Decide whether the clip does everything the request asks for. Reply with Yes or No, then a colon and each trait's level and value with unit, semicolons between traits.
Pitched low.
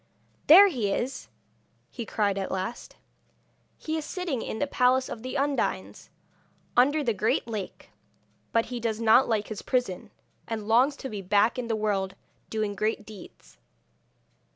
No: high, 225 Hz